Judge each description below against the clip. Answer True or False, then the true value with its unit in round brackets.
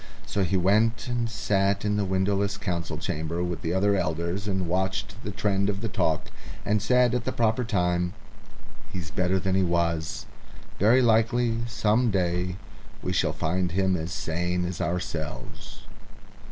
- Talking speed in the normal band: True (160 wpm)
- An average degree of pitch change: True (3.1 semitones)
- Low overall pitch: True (95 Hz)